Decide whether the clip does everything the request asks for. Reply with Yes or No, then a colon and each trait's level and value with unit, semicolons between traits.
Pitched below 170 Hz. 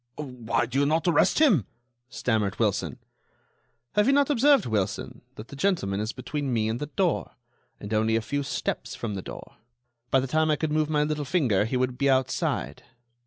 Yes: medium, 140 Hz